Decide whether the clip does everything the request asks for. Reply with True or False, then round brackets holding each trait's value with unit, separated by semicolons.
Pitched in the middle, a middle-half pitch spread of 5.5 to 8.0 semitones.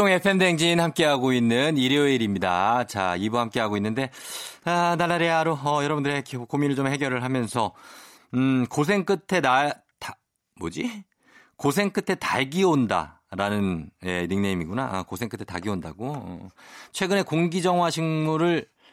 True (145 Hz; 6.8 semitones)